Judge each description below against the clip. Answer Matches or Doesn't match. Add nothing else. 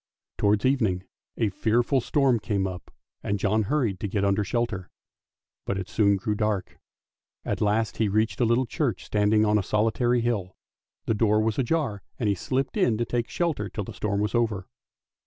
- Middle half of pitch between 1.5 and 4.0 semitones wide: Matches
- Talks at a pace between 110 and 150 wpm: Doesn't match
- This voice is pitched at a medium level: Doesn't match